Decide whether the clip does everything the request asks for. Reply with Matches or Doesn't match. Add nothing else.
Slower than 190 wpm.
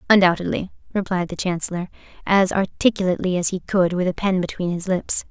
Matches